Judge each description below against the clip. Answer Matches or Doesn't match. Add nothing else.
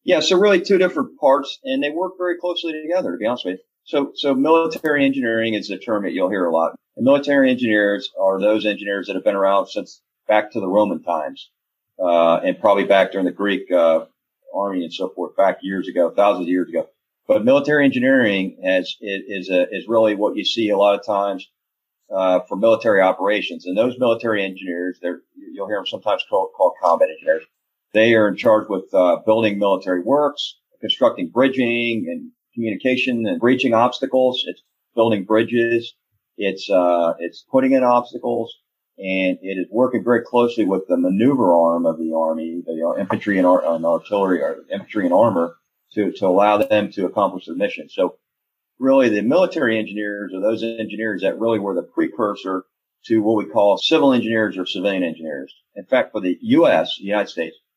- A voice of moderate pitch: Doesn't match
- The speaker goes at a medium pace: Matches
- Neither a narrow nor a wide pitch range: Doesn't match